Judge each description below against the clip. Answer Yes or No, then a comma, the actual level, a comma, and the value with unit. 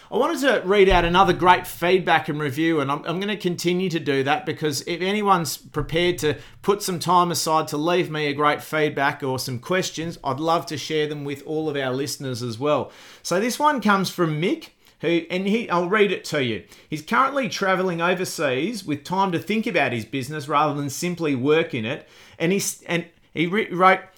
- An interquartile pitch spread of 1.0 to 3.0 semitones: No, average, 3.9 semitones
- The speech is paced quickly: Yes, fast, 210 wpm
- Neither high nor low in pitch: Yes, medium, 165 Hz